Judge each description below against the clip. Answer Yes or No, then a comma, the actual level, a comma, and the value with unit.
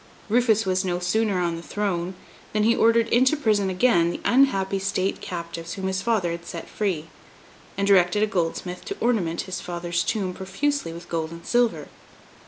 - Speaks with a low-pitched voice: No, high, 190 Hz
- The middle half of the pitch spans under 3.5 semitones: No, average, 4.1 semitones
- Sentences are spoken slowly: No, average, 180 wpm